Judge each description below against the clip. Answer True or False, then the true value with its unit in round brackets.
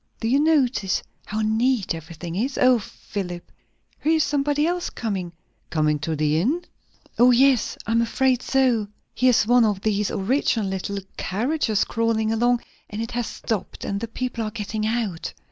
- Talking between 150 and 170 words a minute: True (160 wpm)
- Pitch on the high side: True (225 Hz)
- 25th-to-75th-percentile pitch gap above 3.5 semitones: True (4.2 semitones)